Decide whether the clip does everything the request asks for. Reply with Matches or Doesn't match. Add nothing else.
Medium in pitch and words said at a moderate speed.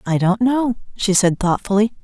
Doesn't match